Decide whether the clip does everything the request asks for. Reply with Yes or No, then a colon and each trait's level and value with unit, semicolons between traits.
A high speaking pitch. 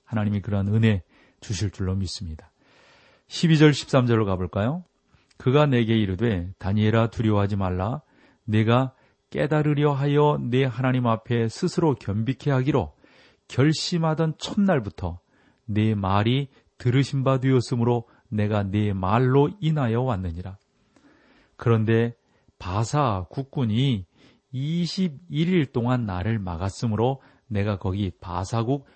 No: low, 120 Hz